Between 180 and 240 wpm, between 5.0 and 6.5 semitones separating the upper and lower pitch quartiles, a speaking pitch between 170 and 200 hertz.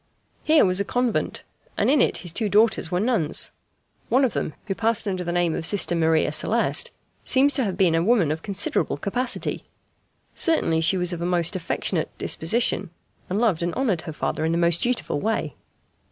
Yes: average, 195 wpm; wide, 5.6 semitones; medium, 185 Hz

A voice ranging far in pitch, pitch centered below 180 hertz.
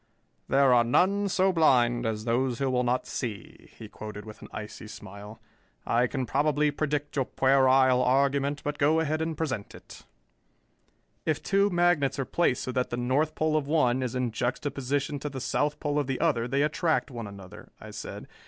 No: average, 3.5 semitones; low, 135 Hz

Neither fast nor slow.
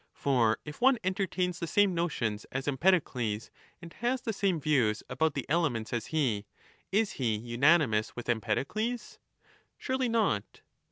Yes: average, 150 wpm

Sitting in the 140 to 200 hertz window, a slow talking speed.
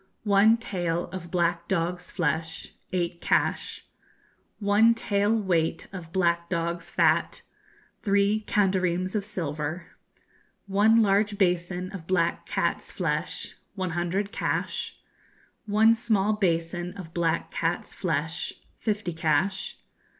Yes: medium, 185 Hz; slow, 115 wpm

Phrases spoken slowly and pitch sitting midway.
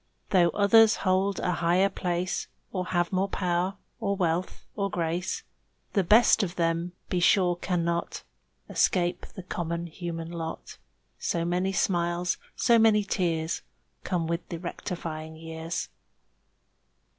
Yes: slow, 130 wpm; medium, 175 Hz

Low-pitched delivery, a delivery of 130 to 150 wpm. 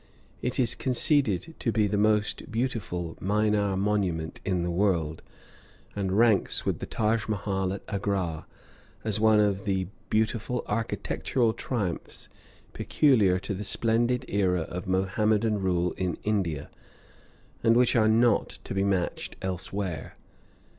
Yes: low, 105 Hz; slow, 135 wpm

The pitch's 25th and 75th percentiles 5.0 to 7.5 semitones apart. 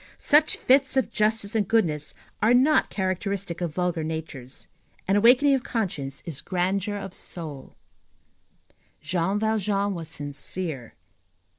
Yes: average, 5.3 semitones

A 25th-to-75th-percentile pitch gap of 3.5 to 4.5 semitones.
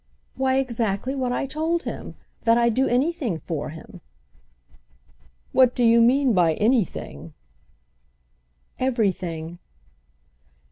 No: wide, 5.4 semitones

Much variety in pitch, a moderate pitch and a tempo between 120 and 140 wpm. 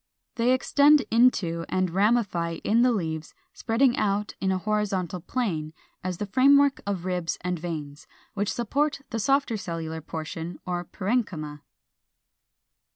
No: wide, 6.1 semitones; high, 195 Hz; slow, 135 wpm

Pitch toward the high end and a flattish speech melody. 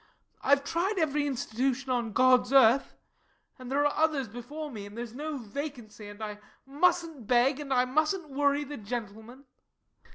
No: very high, 265 Hz; average, 3.6 semitones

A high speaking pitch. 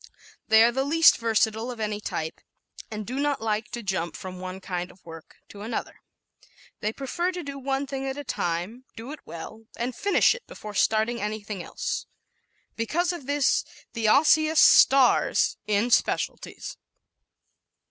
Yes: high, 230 Hz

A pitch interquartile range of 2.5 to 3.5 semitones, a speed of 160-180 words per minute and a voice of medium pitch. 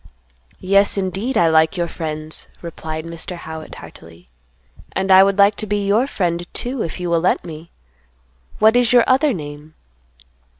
No: average, 4.2 semitones; average, 165 wpm; medium, 180 Hz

